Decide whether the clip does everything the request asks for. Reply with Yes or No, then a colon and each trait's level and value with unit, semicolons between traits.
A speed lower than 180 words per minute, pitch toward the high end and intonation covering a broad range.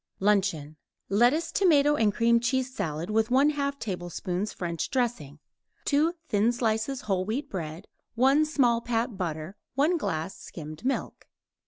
Yes: slow, 135 wpm; high, 225 Hz; wide, 6.7 semitones